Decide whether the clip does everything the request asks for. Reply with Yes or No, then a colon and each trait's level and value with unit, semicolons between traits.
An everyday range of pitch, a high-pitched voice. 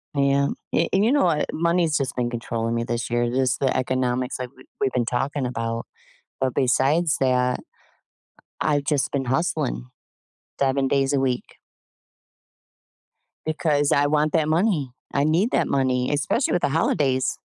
No: average, 3.1 semitones; low, 135 Hz